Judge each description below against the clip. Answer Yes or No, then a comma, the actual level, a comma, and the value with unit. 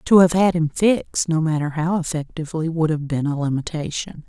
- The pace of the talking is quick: No, average, 195 wpm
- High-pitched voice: No, medium, 160 Hz